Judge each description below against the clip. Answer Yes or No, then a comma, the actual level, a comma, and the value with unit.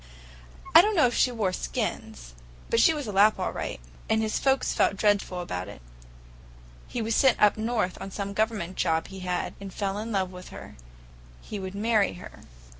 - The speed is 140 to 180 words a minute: No, average, 190 wpm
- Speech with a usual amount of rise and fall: Yes, average, 3.5 semitones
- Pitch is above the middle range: Yes, high, 205 Hz